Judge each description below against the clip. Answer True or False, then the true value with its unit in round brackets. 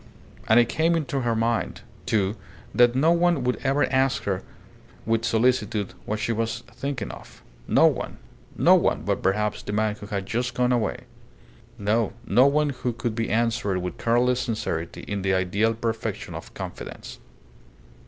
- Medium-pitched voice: False (115 Hz)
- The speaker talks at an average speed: True (165 wpm)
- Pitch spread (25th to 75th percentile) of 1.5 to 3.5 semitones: True (3.0 semitones)